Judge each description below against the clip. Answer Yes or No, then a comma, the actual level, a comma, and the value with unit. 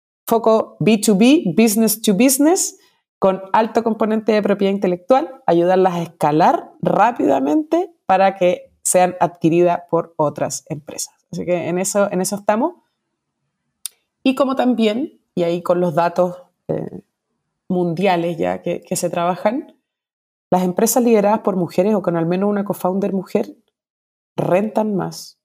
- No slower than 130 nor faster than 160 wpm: Yes, average, 135 wpm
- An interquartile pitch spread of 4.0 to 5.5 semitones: Yes, average, 4.3 semitones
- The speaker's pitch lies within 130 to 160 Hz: No, high, 195 Hz